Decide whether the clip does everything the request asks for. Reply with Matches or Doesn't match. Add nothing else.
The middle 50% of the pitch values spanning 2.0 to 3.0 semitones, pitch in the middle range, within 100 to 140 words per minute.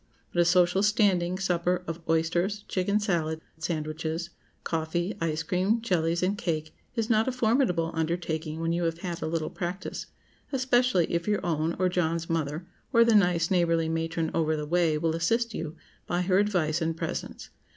Doesn't match